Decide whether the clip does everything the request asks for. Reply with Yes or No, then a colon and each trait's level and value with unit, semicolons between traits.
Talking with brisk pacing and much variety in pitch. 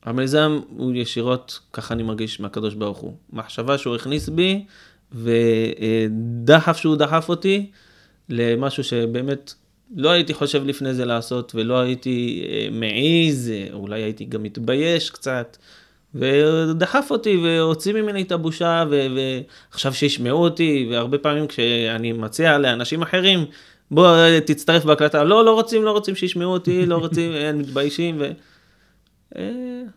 No: average, 125 wpm; wide, 6.0 semitones